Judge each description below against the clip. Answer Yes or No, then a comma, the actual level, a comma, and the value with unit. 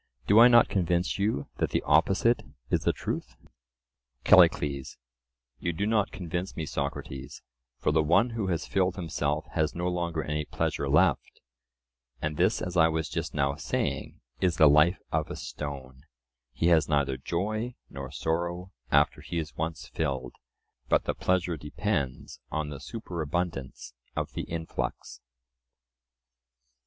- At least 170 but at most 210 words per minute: No, average, 145 wpm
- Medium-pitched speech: No, very low, 80 Hz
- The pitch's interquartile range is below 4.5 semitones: Yes, average, 3.6 semitones